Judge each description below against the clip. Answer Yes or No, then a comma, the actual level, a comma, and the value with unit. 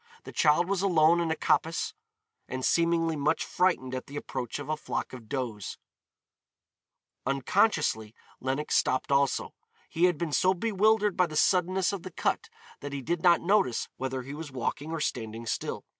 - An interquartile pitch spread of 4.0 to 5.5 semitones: Yes, average, 5.1 semitones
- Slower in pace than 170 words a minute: No, average, 175 wpm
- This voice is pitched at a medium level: Yes, medium, 155 Hz